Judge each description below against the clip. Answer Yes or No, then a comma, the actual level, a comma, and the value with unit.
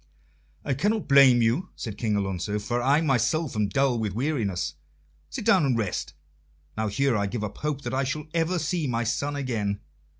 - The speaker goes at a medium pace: Yes, average, 190 wpm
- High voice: No, low, 120 Hz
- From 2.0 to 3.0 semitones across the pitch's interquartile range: No, average, 5.1 semitones